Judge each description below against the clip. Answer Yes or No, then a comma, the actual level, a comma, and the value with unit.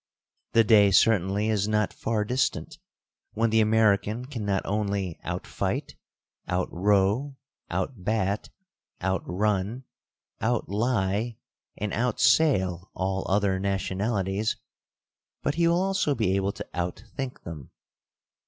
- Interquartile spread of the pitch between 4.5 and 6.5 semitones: No, average, 3.3 semitones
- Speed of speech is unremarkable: No, slow, 125 wpm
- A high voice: No, low, 105 Hz